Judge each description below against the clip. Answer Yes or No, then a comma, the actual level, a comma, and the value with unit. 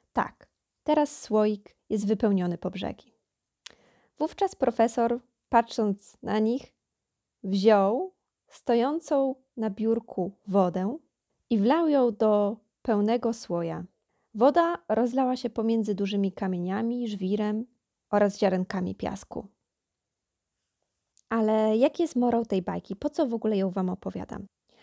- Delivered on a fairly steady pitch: No, average, 3.8 semitones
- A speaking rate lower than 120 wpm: Yes, slow, 110 wpm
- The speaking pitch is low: No, high, 220 Hz